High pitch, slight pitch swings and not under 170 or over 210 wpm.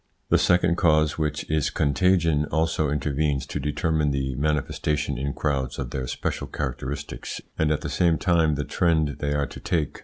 No: very low, 75 Hz; narrow, 2.0 semitones; average, 175 wpm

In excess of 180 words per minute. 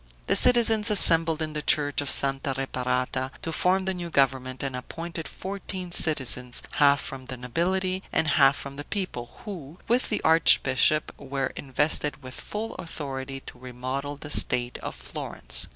No: average, 160 wpm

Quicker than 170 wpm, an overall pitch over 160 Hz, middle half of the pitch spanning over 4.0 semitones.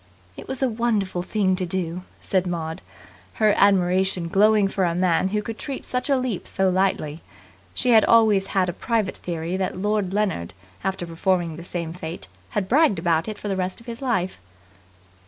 No: average, 190 wpm; high, 190 Hz; average, 3.3 semitones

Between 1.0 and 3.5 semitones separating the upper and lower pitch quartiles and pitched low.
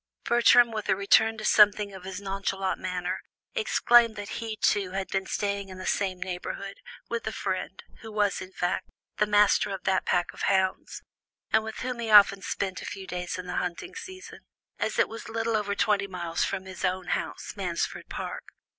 No: average, 2.7 semitones; high, 200 Hz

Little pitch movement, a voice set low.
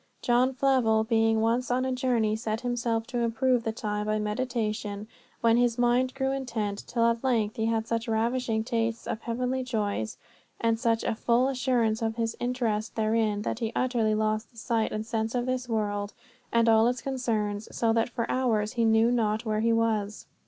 No: narrow, 1.9 semitones; high, 230 Hz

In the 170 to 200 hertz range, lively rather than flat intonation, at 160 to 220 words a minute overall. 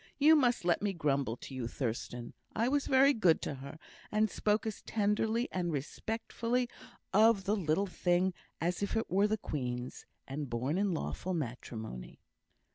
Yes: medium, 185 Hz; wide, 7.9 semitones; average, 165 wpm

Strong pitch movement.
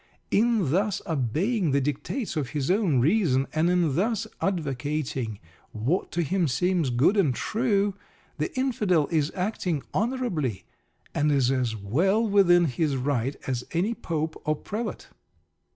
Yes: wide, 6.5 semitones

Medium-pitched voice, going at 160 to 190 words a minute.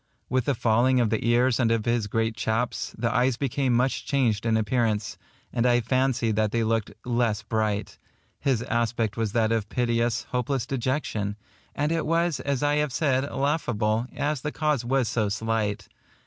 No: low, 120 Hz; average, 175 wpm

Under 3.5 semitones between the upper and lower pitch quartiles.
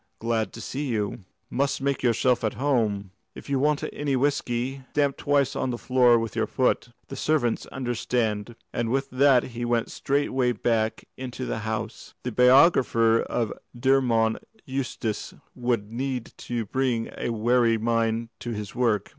Yes: average, 2.7 semitones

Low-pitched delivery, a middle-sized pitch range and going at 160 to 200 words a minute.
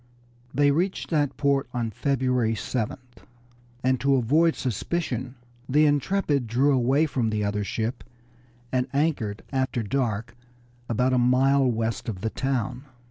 No: low, 130 Hz; average, 3.4 semitones; slow, 135 wpm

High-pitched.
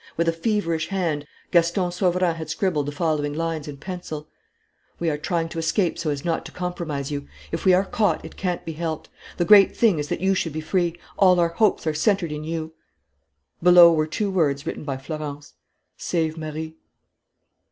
No: medium, 165 Hz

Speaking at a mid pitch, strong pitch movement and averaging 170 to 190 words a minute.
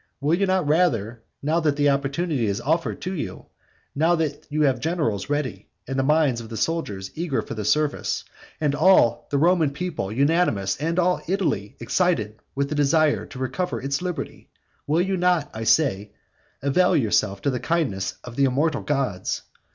Yes: medium, 145 Hz; wide, 5.8 semitones; average, 180 wpm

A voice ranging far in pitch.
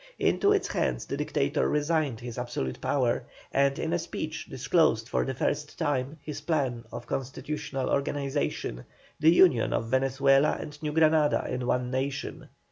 No: average, 3.1 semitones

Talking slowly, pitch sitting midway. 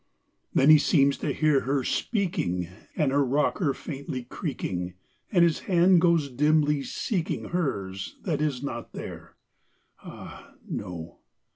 Yes: slow, 130 wpm; medium, 145 Hz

